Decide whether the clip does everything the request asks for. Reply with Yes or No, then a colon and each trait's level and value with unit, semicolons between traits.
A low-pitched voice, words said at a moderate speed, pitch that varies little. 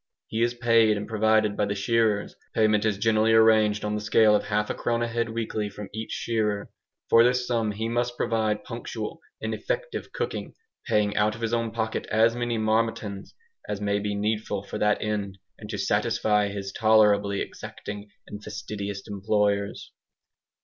Yes: low, 110 Hz; average, 175 wpm; narrow, 1.7 semitones